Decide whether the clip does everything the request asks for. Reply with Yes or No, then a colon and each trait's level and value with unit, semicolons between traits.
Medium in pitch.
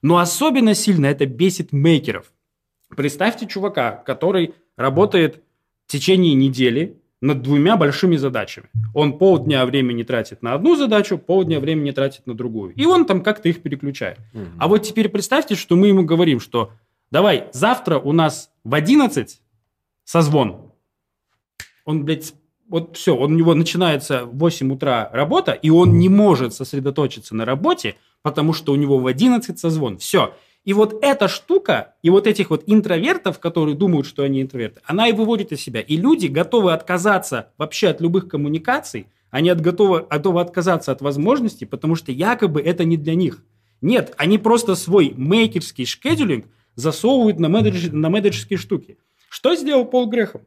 Yes: medium, 165 Hz